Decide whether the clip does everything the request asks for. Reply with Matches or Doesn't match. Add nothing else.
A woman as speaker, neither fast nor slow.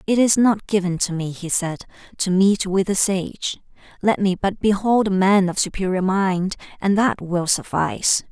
Matches